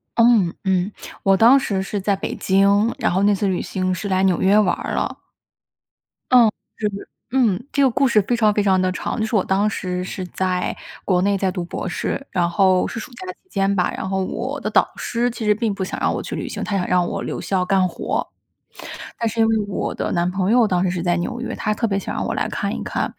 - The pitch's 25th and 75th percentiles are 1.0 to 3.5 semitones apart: Yes, average, 3.2 semitones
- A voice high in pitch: Yes, high, 195 Hz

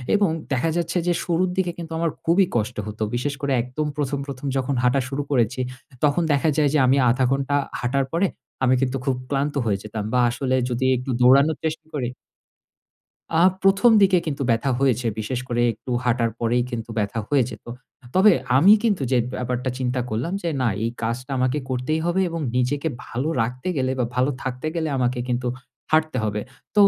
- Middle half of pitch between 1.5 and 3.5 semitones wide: No, average, 4.1 semitones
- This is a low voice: Yes, low, 130 Hz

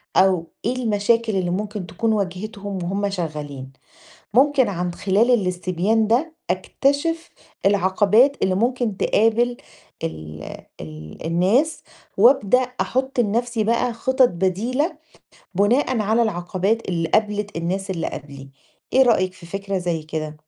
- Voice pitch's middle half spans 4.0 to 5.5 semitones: Yes, average, 4.9 semitones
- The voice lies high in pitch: Yes, high, 205 Hz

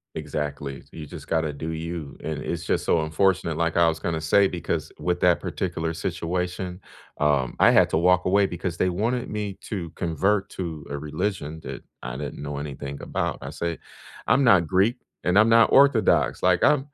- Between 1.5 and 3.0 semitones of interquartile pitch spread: No, average, 3.5 semitones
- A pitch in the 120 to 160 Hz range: No, very low, 85 Hz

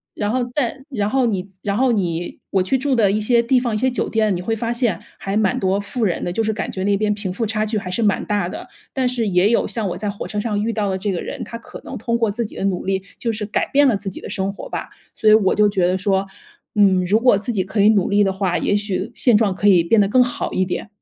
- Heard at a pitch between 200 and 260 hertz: Yes, high, 210 Hz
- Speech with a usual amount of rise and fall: Yes, average, 3.0 semitones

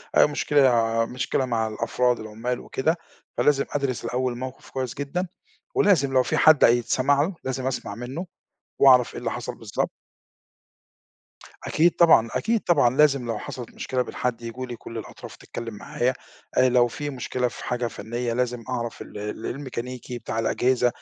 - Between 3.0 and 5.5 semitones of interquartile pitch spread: No, narrow, 2.4 semitones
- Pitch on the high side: No, low, 125 Hz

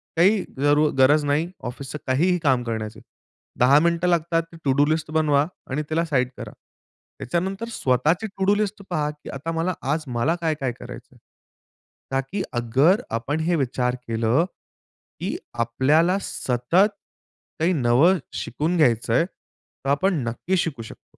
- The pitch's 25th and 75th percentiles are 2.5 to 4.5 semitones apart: No, average, 4.9 semitones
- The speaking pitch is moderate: Yes, medium, 150 Hz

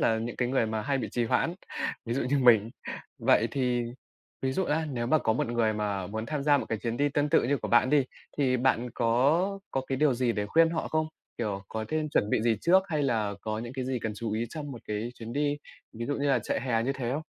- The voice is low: Yes, low, 125 Hz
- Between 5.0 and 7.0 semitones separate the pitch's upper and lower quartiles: No, average, 4.2 semitones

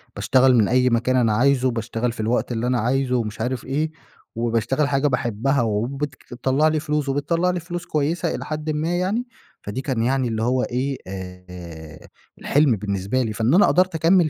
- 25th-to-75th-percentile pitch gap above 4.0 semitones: Yes, average, 4.7 semitones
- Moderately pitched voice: No, low, 130 Hz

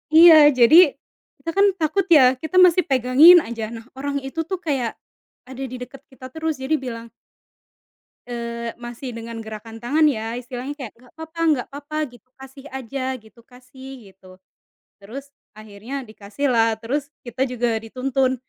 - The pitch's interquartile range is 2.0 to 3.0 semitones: No, average, 3.5 semitones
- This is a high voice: Yes, very high, 255 Hz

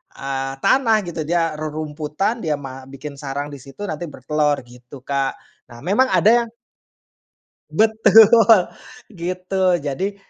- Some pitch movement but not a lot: No, wide, 6.2 semitones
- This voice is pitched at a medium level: Yes, medium, 155 Hz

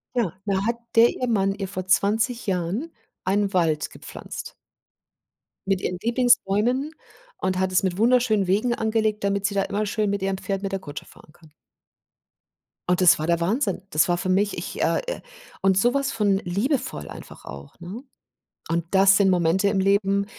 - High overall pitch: Yes, high, 195 Hz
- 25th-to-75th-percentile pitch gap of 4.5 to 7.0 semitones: No, average, 2.9 semitones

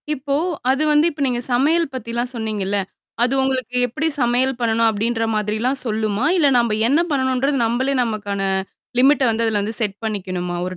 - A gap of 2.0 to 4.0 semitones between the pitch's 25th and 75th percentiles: Yes, average, 3.7 semitones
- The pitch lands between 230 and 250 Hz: Yes, high, 235 Hz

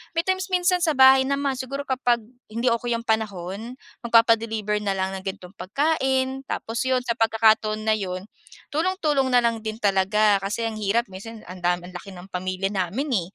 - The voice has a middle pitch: No, high, 225 Hz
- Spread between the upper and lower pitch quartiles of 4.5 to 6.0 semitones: Yes, average, 5.0 semitones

